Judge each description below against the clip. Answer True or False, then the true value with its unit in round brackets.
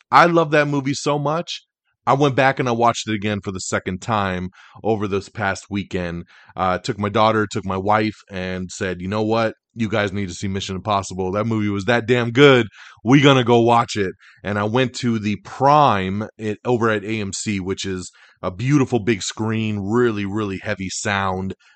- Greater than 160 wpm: True (200 wpm)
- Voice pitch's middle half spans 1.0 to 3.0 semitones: False (3.6 semitones)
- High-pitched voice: False (105 Hz)